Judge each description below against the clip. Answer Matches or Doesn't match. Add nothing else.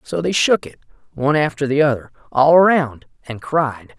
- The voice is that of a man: Matches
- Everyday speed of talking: Matches